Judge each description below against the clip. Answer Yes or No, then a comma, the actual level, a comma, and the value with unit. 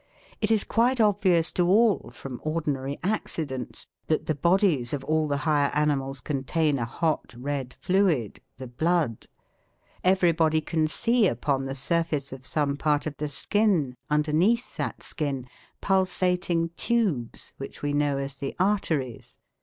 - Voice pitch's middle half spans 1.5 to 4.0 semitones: No, average, 4.7 semitones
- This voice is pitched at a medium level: Yes, medium, 155 Hz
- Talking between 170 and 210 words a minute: No, average, 145 wpm